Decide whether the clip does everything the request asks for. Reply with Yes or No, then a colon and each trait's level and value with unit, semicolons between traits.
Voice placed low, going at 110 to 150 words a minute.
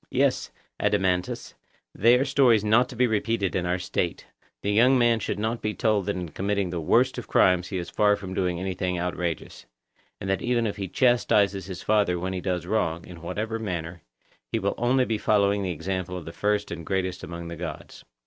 No: very low, 95 Hz; fast, 205 wpm